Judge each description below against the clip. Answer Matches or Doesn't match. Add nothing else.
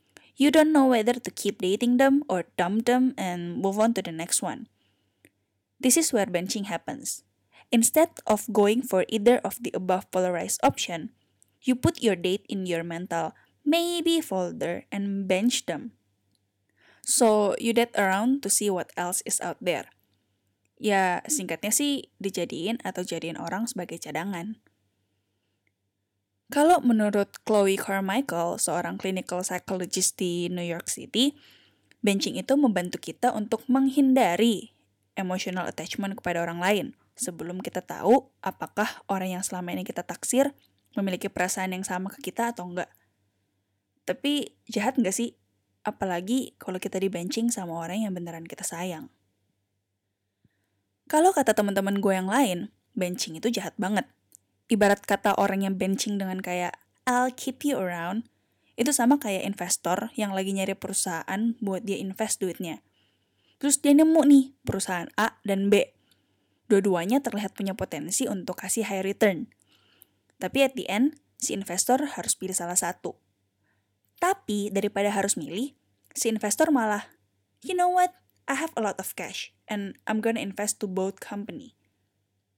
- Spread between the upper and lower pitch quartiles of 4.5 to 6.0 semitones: Matches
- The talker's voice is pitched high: Matches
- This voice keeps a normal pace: Doesn't match